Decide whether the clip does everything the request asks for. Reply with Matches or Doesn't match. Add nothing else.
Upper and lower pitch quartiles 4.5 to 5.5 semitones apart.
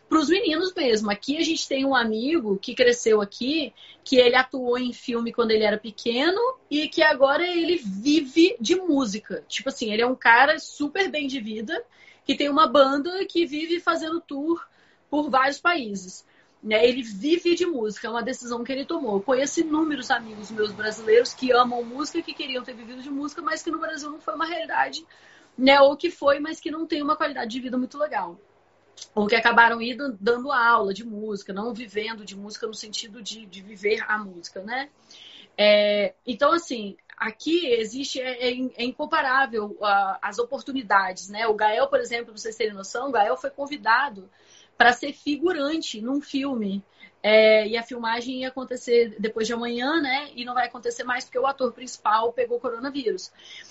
Matches